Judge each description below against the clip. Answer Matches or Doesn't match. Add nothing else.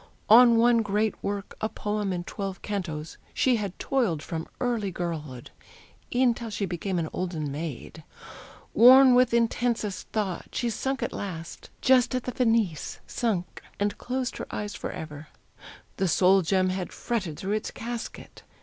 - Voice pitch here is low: Doesn't match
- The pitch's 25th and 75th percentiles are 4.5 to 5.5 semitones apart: Matches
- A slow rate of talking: Doesn't match